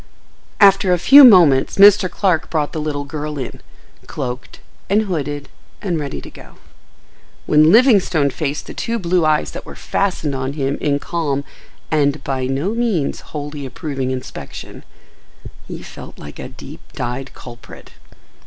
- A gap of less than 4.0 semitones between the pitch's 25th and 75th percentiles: No, average, 4.9 semitones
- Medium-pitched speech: Yes, medium, 150 Hz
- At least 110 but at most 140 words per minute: No, average, 150 wpm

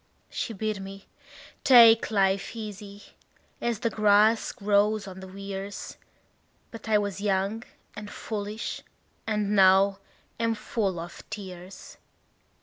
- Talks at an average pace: No, slow, 120 wpm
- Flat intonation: Yes, narrow, 1.8 semitones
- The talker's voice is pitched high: Yes, high, 205 Hz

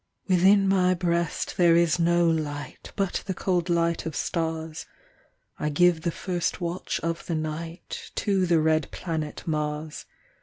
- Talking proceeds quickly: No, average, 150 wpm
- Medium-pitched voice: Yes, medium, 170 Hz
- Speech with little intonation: Yes, narrow, 2.0 semitones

